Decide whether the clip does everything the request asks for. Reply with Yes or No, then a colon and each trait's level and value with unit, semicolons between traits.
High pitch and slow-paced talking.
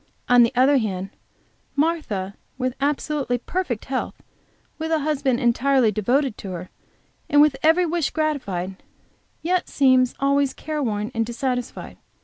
Yes: very high, 260 Hz; slow, 130 wpm